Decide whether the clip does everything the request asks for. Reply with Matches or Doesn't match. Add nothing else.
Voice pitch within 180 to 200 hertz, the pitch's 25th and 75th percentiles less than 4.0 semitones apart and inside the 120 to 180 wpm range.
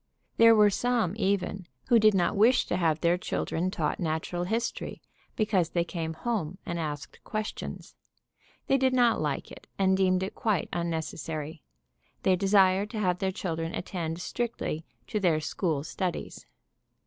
Doesn't match